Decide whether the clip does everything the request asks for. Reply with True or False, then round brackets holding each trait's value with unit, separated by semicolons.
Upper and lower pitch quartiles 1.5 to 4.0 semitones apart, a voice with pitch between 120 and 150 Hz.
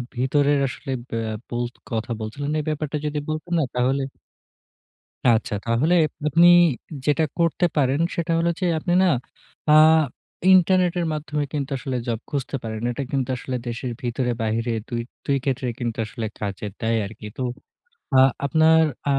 False (4.6 semitones; 135 Hz)